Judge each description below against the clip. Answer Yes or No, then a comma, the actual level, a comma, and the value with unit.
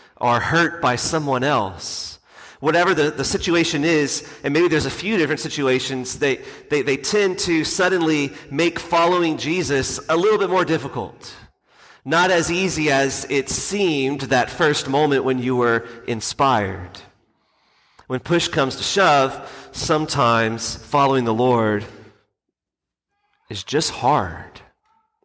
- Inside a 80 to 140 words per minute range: Yes, slow, 135 wpm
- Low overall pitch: No, medium, 145 Hz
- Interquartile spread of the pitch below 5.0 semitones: No, average, 5.3 semitones